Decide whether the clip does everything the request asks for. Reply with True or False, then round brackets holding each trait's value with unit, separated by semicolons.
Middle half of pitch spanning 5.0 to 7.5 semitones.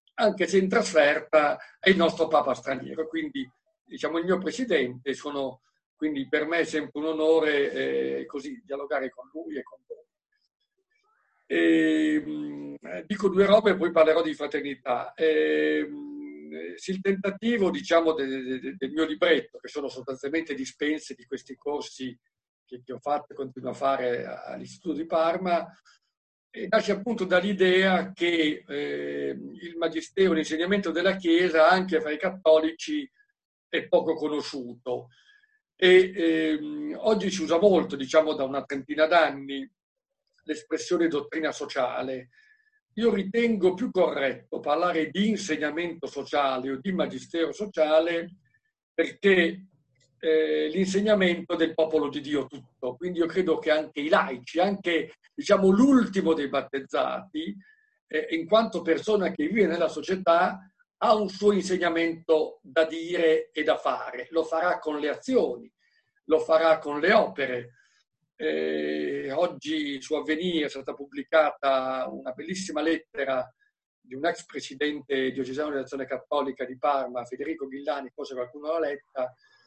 True (5.3 semitones)